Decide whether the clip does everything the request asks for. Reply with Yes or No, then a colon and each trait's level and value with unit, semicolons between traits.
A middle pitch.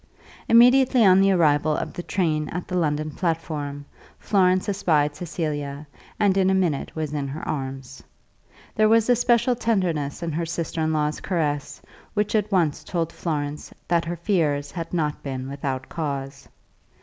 Yes: medium, 165 Hz